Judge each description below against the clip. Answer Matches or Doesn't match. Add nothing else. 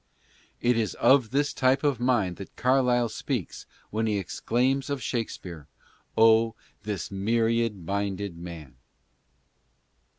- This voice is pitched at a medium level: Doesn't match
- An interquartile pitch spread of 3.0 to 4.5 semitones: Matches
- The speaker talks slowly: Matches